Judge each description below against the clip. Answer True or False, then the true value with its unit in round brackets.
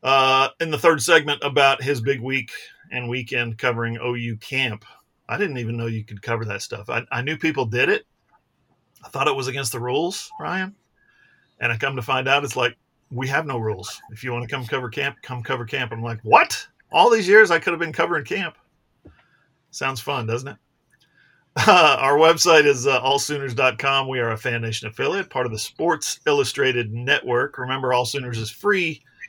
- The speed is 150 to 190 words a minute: False (200 wpm)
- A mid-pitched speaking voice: False (130 Hz)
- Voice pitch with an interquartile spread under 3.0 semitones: False (3.3 semitones)